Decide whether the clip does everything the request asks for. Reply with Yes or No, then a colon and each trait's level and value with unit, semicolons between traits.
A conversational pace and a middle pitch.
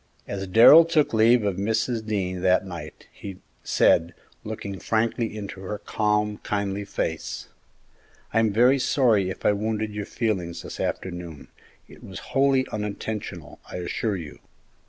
No: average, 145 wpm; low, 105 Hz